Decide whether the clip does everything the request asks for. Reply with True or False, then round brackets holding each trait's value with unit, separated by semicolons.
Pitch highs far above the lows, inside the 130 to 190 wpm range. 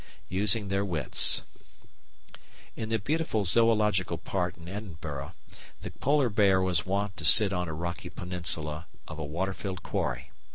False (3.5 semitones; 150 wpm)